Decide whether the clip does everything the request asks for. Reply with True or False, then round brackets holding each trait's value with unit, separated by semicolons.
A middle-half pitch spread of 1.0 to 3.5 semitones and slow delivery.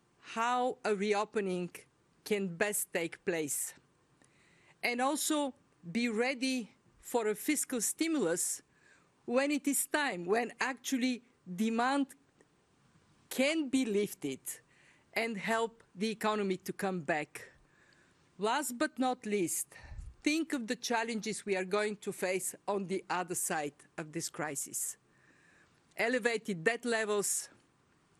False (4.8 semitones; 115 wpm)